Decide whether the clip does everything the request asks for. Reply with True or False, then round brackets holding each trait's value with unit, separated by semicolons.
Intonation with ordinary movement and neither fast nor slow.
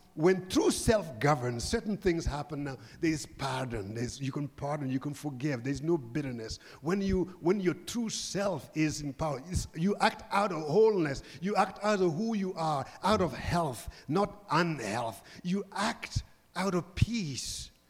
False (5.9 semitones; 175 wpm)